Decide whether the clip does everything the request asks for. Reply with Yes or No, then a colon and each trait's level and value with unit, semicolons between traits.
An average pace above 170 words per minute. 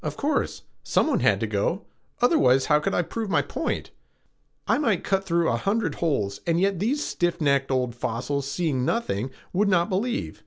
Yes: average, 185 wpm